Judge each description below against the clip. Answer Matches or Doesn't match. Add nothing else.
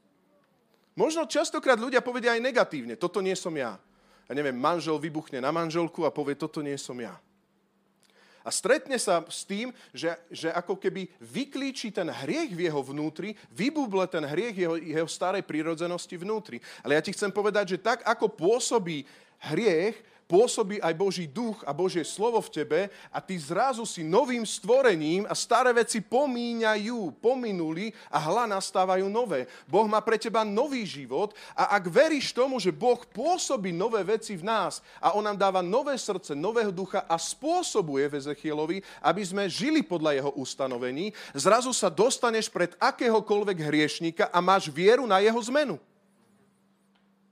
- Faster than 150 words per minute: Matches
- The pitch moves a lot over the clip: Matches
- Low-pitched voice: Doesn't match